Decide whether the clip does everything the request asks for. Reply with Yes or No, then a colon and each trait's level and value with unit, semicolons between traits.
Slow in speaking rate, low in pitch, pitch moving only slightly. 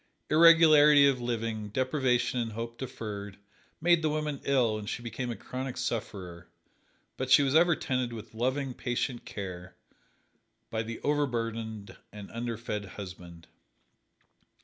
No: slow, 130 wpm; low, 120 Hz; average, 4.2 semitones